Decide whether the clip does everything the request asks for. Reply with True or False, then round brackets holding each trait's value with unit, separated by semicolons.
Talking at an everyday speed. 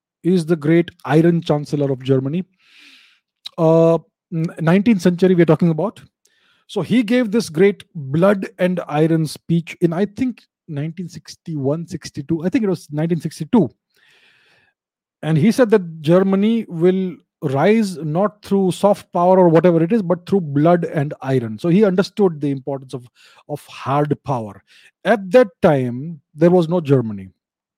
True (150 wpm)